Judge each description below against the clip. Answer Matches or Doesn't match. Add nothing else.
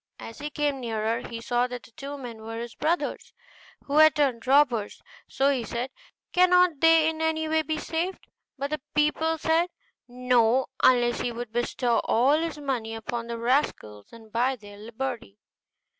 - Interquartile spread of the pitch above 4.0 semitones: Matches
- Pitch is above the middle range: Matches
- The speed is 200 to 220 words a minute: Doesn't match